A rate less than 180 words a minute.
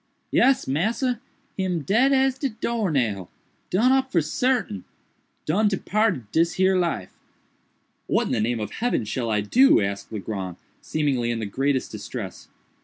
Yes: average, 140 wpm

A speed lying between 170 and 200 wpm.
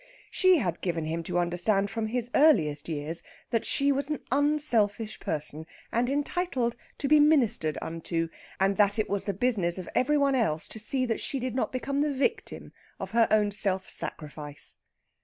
Yes: average, 180 wpm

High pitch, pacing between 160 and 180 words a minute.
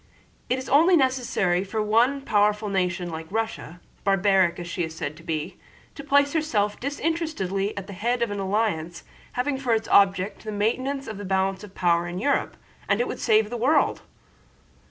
Yes: high, 210 Hz; average, 175 wpm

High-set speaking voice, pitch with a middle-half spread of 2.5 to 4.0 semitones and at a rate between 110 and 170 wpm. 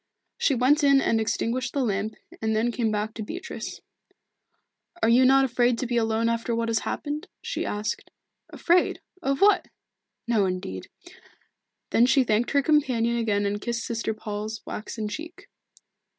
Yes: high, 235 Hz; average, 3.6 semitones; average, 160 wpm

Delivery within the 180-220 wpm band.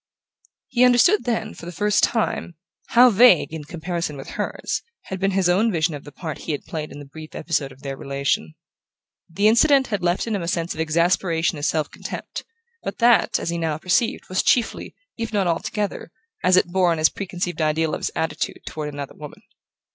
Yes: fast, 205 wpm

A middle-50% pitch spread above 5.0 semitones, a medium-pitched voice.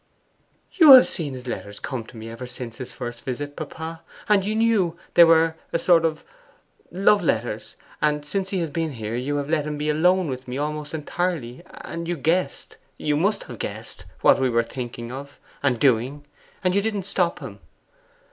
Yes: wide, 5.5 semitones; medium, 150 Hz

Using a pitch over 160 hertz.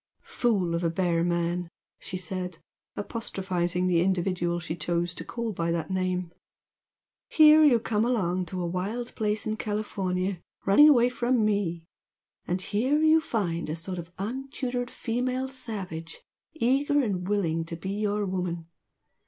Yes: high, 190 Hz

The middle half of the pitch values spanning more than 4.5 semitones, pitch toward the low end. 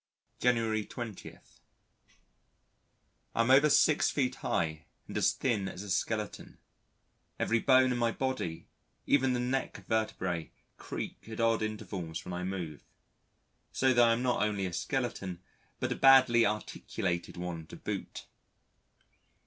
Yes: average, 5.2 semitones; low, 110 Hz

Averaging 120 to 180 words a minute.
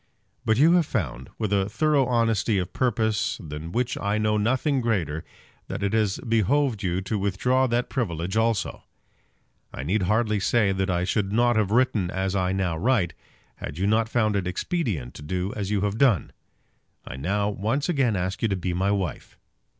No: average, 190 wpm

